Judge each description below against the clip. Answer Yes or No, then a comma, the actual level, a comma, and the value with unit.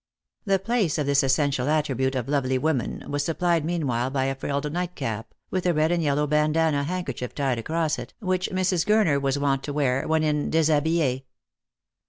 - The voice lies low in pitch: No, medium, 150 Hz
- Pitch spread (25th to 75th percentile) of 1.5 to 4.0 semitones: Yes, average, 3.5 semitones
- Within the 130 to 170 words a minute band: No, average, 180 wpm